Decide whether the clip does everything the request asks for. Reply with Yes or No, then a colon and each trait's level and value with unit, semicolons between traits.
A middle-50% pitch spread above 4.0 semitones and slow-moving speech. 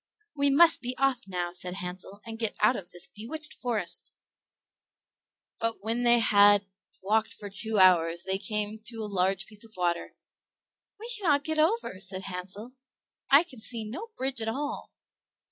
No: average, 4.9 semitones; average, 165 wpm